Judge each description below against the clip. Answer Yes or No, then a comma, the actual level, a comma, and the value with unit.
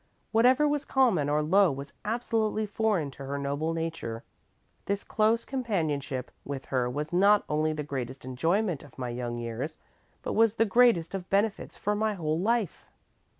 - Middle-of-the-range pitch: Yes, medium, 165 Hz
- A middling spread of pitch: No, wide, 7.4 semitones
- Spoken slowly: No, average, 165 wpm